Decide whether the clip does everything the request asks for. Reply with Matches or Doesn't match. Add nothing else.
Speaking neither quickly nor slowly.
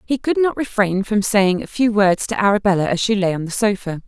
Doesn't match